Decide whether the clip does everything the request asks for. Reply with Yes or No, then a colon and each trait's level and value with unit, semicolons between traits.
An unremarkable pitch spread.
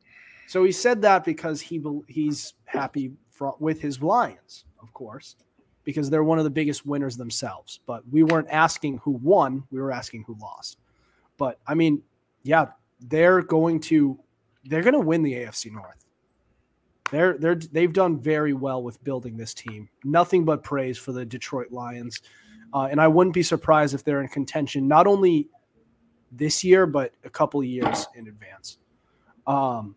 Yes: average, 4.3 semitones